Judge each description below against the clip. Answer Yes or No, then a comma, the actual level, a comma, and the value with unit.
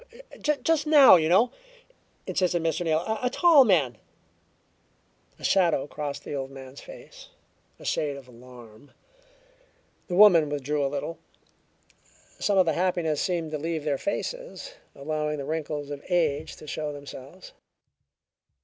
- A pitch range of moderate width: Yes, average, 4.3 semitones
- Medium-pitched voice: Yes, medium, 155 Hz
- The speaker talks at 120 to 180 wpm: Yes, average, 140 wpm